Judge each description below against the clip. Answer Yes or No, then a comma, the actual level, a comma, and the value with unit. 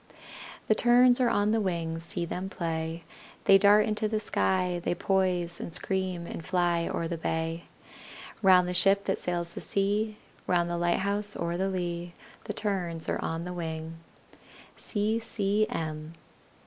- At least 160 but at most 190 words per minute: No, average, 150 wpm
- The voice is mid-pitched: Yes, medium, 180 Hz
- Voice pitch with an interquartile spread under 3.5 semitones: Yes, average, 2.7 semitones